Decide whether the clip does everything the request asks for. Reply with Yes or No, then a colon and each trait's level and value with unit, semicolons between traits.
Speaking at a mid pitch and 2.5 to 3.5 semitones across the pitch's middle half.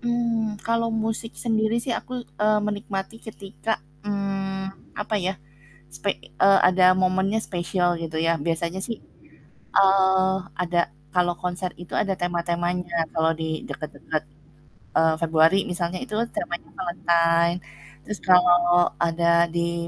Yes: medium, 180 Hz; average, 3.2 semitones